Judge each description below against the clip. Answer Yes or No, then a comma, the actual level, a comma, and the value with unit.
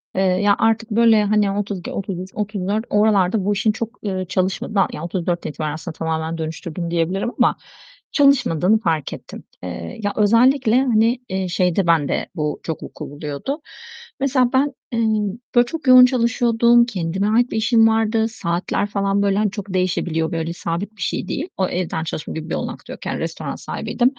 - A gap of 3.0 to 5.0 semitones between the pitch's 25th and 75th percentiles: Yes, average, 4.7 semitones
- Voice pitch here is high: Yes, high, 200 Hz